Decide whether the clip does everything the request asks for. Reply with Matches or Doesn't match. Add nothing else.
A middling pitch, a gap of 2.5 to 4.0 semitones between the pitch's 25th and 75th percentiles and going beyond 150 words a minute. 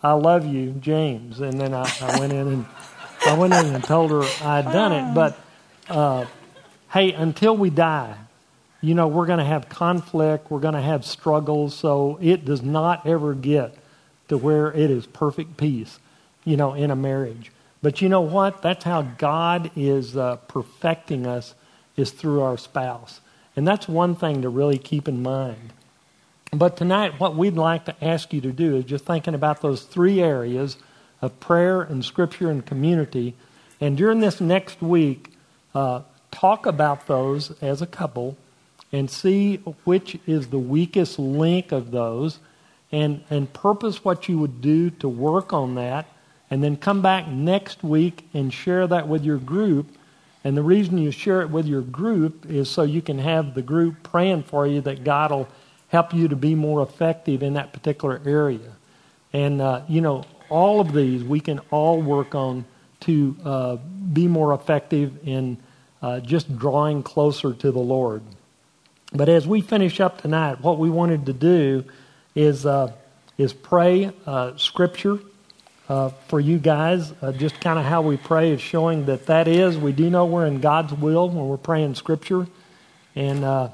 Matches